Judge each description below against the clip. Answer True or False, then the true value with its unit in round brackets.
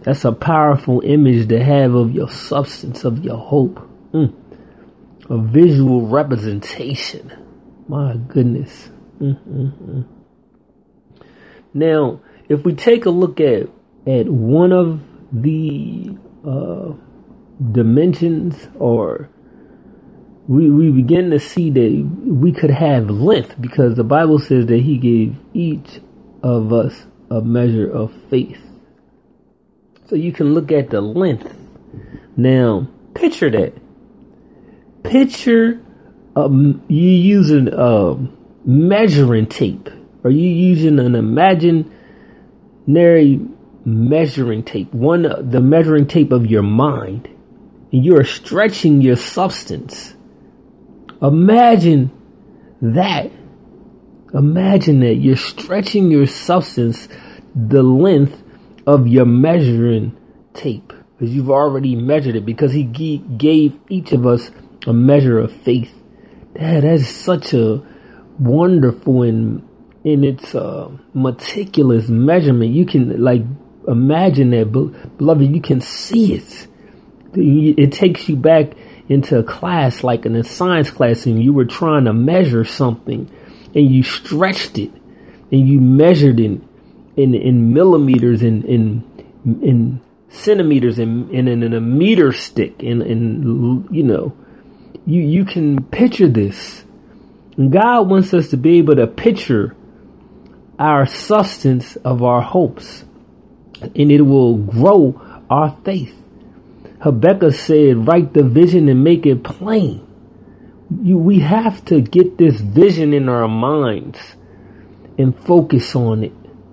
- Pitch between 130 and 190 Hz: True (140 Hz)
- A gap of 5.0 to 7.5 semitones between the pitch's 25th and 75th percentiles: True (5.3 semitones)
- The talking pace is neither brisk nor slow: False (120 wpm)